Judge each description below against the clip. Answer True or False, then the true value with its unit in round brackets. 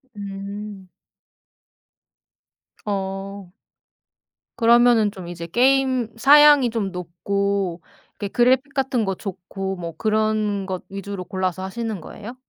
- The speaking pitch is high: True (200 Hz)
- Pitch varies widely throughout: False (3.5 semitones)